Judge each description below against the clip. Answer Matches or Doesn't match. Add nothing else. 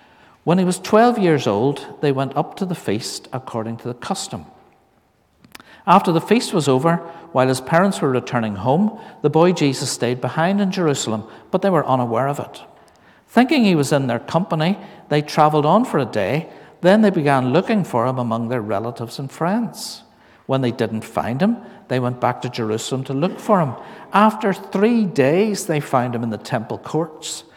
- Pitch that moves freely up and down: Matches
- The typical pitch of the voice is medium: Matches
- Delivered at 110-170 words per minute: Doesn't match